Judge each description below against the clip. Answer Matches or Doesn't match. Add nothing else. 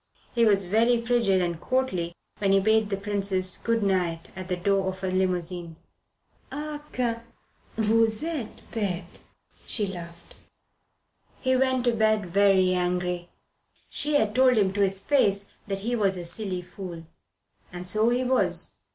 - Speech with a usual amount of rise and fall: Matches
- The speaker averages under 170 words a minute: Matches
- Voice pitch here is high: Matches